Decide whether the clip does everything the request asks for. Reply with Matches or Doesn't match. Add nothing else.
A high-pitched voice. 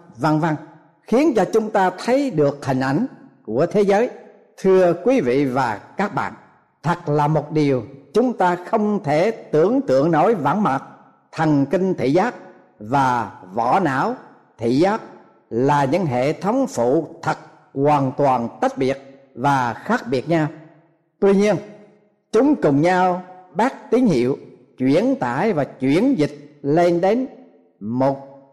Doesn't match